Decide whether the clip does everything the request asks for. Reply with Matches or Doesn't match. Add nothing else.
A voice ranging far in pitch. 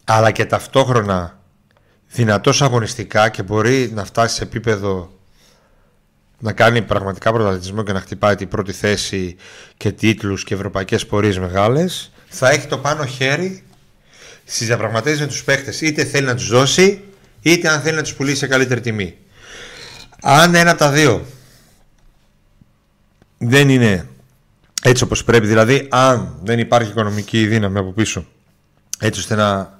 Doesn't match